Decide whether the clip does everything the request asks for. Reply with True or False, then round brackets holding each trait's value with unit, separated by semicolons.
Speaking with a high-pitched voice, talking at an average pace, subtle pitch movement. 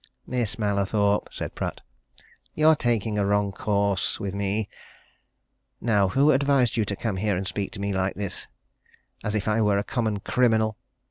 False (105 Hz; 165 wpm; 2.2 semitones)